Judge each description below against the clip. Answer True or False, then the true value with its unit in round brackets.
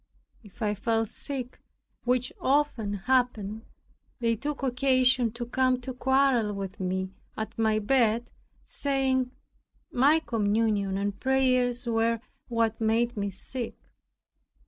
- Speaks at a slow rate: True (120 wpm)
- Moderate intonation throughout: True (3.2 semitones)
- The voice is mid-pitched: False (235 Hz)